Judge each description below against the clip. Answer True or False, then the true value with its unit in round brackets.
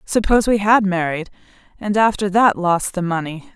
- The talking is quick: False (170 wpm)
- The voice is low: False (195 Hz)